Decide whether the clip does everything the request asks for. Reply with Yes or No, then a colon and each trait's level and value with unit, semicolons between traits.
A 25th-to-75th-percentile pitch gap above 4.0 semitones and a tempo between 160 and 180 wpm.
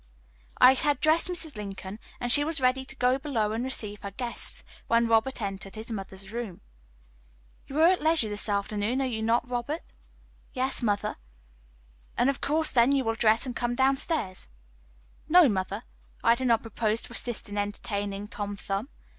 Yes: average, 4.4 semitones; average, 175 wpm